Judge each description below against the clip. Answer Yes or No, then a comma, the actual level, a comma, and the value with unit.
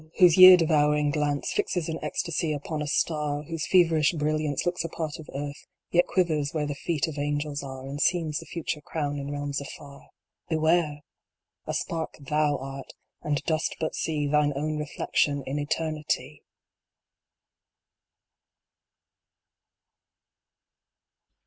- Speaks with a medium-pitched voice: Yes, medium, 150 Hz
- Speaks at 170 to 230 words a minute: No, slow, 135 wpm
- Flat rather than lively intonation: Yes, narrow, 1.8 semitones